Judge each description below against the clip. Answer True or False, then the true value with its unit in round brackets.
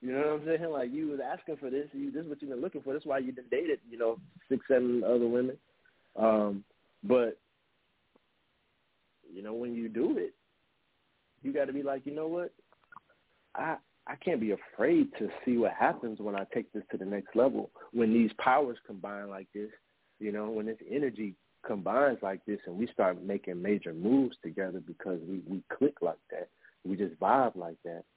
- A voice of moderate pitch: False (115 Hz)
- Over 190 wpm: True (200 wpm)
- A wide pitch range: True (5.8 semitones)